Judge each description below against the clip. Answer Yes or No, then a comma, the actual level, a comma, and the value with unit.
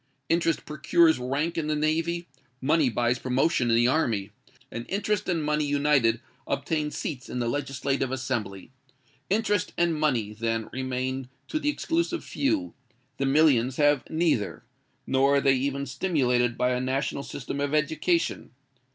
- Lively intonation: No, average, 4.2 semitones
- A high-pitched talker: No, medium, 140 Hz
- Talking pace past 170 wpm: No, average, 140 wpm